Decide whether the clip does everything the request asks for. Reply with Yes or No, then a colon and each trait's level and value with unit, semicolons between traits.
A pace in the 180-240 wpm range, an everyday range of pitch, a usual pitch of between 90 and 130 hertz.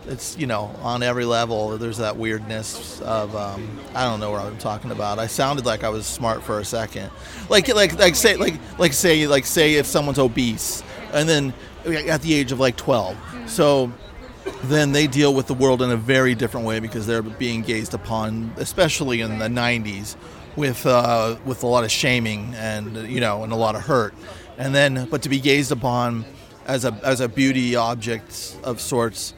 Yes: average, 200 wpm; average, 3.4 semitones; low, 120 Hz